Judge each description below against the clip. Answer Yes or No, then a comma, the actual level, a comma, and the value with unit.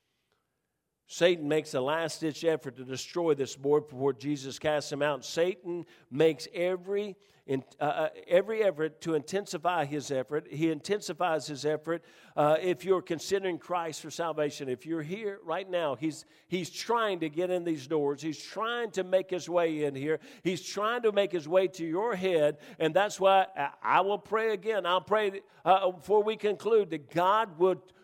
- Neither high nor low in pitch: Yes, medium, 170 Hz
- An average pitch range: Yes, average, 3.8 semitones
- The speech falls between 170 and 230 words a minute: Yes, average, 175 wpm